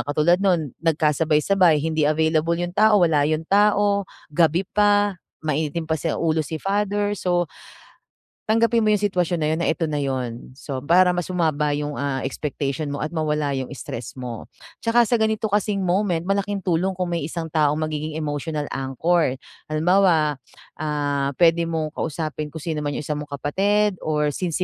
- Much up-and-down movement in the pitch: No, average, 3.8 semitones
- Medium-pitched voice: Yes, medium, 160 Hz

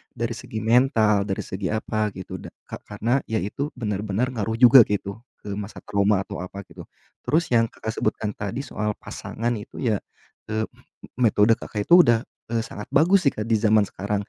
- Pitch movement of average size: No, narrow, 2.3 semitones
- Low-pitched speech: Yes, low, 110 Hz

